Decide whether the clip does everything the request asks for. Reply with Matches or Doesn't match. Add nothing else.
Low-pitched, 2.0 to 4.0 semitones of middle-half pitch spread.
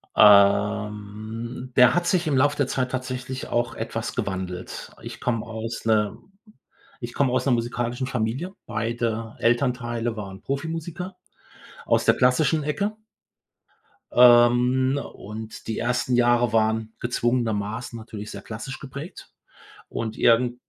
Matches